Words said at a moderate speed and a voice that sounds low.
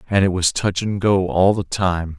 No: fast, 245 wpm; very low, 95 Hz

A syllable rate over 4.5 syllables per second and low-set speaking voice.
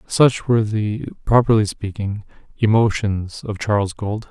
No: 4.4 syllables/s; low, 105 Hz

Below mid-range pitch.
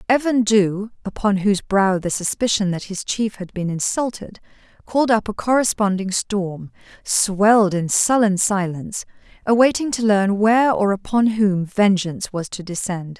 No: high, 205 Hz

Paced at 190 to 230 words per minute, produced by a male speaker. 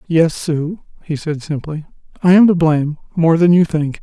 No: average, 180 wpm; male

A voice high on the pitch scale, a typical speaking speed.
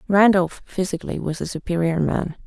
No: medium, 180 Hz; average, 145 wpm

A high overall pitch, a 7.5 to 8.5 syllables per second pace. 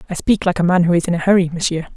No: medium, 175 Hz; 7.9 syllables/s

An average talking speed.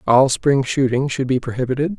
Yes: average, 180 wpm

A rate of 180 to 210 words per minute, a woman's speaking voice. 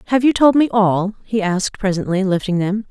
Yes: fast, 205 wpm; female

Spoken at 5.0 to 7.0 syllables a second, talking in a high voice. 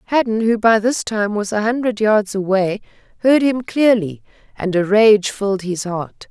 No: 4.5 syllables/s; high, 210 Hz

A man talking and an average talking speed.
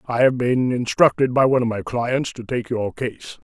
No: male; fast, 220 wpm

